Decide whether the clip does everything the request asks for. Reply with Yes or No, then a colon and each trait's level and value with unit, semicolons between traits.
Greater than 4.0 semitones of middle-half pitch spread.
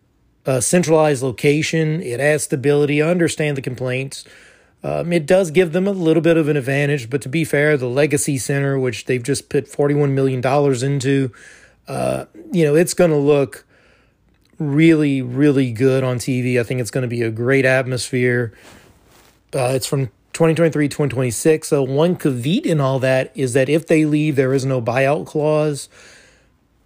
No: average, 2.9 semitones